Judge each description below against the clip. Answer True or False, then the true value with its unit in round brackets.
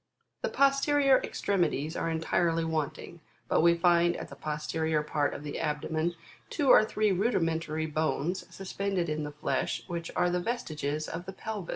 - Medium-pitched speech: True (170 Hz)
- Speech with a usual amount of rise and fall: True (3.5 semitones)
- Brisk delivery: False (165 wpm)